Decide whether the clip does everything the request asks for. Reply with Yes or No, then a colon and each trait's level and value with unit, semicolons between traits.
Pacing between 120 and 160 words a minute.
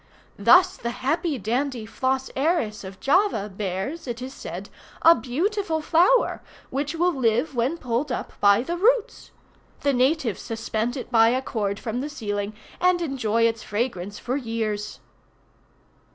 Yes: average, 150 wpm